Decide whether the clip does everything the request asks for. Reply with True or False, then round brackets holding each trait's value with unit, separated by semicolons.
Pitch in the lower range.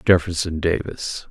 True (85 Hz)